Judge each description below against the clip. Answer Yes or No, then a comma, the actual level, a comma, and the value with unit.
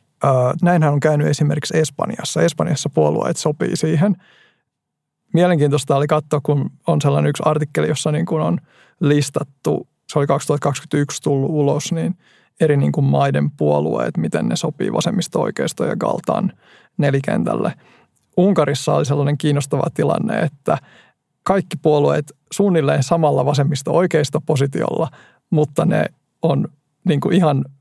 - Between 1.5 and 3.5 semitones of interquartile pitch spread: Yes, narrow, 2.5 semitones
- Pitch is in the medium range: Yes, medium, 150 Hz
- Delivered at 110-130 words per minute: Yes, average, 125 wpm